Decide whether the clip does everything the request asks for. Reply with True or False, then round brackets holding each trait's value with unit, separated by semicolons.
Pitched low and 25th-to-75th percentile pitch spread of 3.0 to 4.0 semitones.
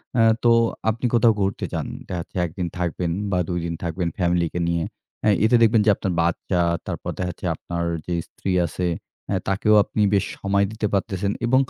True (95 Hz; 3.5 semitones)